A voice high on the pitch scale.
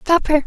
Yes: very high, 315 Hz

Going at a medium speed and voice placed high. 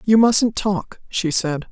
Yes: average, 175 wpm; high, 195 Hz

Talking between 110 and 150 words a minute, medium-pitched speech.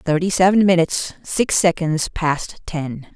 Yes: slow, 135 wpm; medium, 170 Hz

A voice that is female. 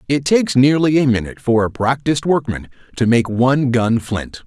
No: male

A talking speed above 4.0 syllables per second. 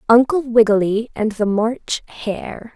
No: 3.9 syllables/s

